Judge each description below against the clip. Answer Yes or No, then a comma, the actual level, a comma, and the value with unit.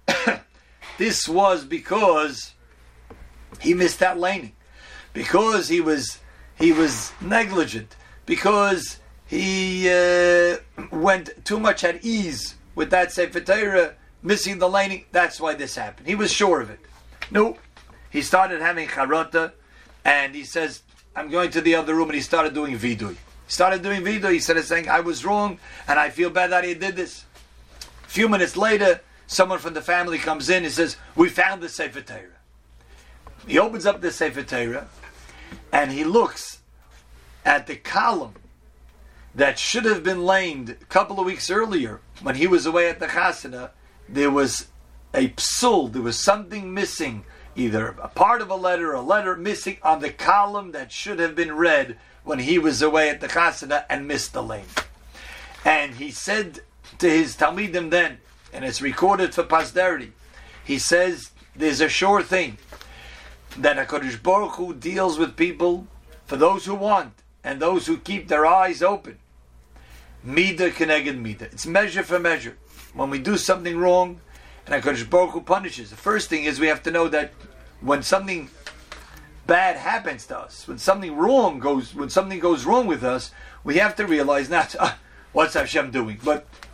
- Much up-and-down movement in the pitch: Yes, wide, 6.4 semitones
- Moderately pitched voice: Yes, medium, 165 Hz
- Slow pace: No, average, 165 wpm